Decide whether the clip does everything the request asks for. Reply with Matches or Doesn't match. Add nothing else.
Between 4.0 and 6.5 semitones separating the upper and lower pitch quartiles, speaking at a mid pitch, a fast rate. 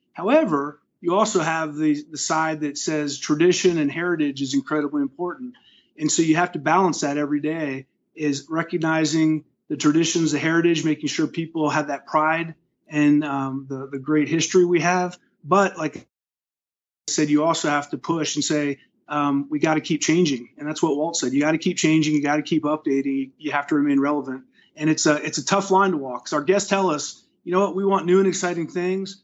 Doesn't match